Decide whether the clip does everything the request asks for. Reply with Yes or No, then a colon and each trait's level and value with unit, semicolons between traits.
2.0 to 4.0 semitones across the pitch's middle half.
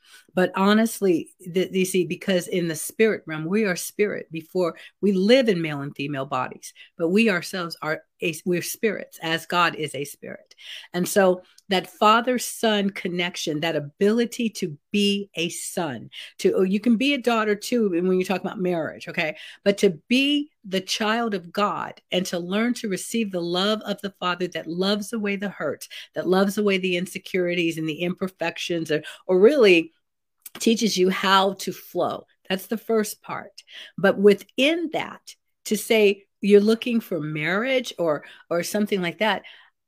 Yes: average, 3.6 semitones